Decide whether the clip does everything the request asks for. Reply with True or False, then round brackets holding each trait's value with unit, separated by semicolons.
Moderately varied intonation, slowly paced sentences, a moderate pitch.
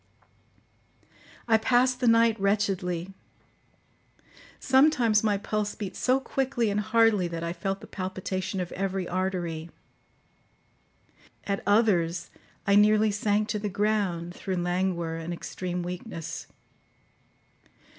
False (3.3 semitones; 115 wpm; 195 Hz)